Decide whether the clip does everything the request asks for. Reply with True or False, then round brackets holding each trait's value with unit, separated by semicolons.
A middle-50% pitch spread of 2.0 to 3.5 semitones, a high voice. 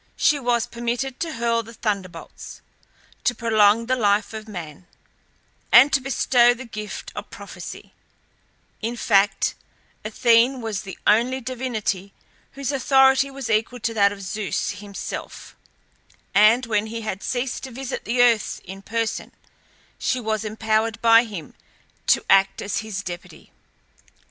True (2.9 semitones; 230 Hz)